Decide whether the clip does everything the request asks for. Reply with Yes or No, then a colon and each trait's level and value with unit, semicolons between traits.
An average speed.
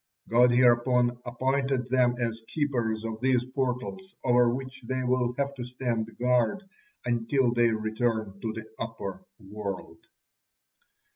No: slow, 130 wpm